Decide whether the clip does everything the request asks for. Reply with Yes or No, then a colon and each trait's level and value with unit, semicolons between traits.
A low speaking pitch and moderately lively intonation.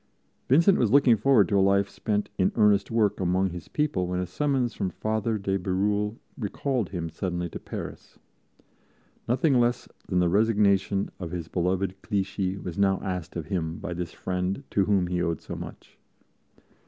Yes: low, 100 Hz; average, 3.1 semitones